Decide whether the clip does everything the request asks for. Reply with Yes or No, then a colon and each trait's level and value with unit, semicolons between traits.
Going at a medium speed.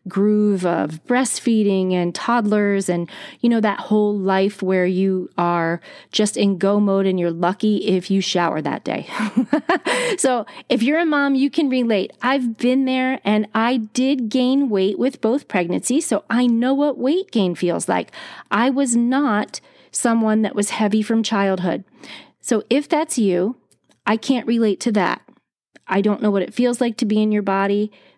Yes: average, 175 wpm